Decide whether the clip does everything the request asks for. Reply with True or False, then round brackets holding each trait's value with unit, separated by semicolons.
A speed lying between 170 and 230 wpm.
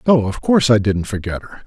False (250 wpm)